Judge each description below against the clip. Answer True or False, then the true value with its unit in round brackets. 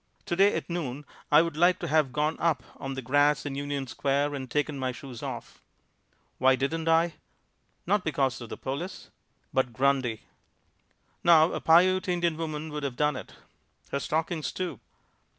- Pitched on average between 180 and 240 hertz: False (150 Hz)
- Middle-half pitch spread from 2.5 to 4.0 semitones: True (3.5 semitones)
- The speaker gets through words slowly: False (170 wpm)